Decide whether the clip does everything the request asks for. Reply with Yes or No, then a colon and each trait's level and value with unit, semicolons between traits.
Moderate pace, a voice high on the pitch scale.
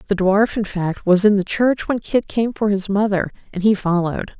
No: fast, 230 wpm; high, 200 Hz